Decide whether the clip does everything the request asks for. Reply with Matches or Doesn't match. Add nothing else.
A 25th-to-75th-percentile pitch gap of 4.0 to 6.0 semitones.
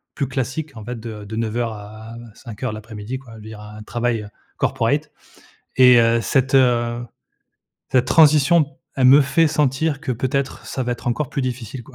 Doesn't match